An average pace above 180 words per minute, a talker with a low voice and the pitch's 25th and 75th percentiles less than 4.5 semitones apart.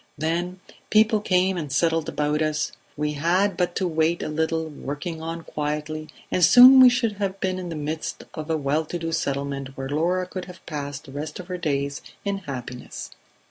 No: average, 195 wpm; medium, 160 Hz; average, 3.5 semitones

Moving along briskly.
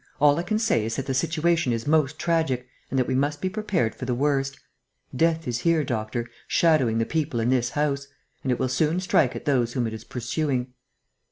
Yes: fast, 215 wpm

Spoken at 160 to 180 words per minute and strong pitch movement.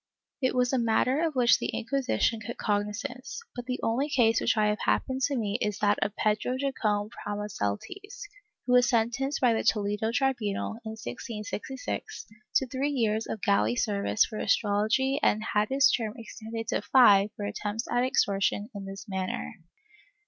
No: average, 170 wpm; average, 3.6 semitones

